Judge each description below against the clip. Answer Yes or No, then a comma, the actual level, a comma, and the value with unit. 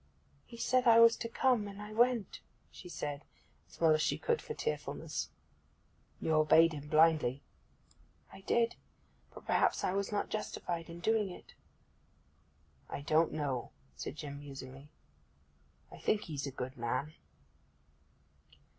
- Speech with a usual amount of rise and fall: No, wide, 6.8 semitones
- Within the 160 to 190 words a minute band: No, average, 145 wpm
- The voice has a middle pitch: Yes, medium, 165 Hz